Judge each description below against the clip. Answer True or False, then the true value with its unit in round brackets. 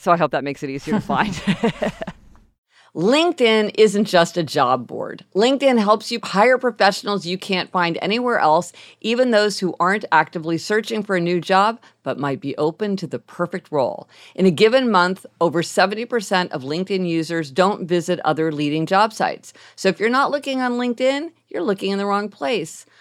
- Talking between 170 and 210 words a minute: True (185 wpm)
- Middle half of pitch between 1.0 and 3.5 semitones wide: False (4.3 semitones)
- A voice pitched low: False (190 Hz)